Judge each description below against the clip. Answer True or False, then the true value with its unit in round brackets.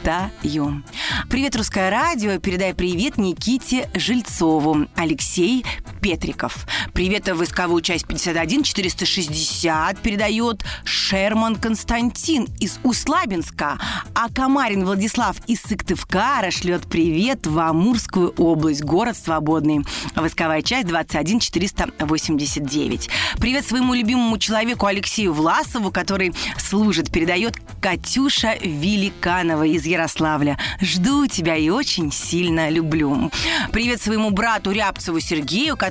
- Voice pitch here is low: False (185 Hz)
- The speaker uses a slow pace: True (95 wpm)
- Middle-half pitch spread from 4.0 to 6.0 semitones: True (5.5 semitones)